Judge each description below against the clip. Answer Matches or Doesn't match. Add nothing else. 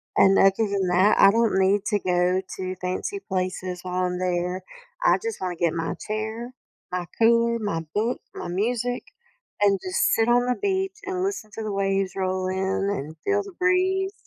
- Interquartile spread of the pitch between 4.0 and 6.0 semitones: Matches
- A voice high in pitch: Matches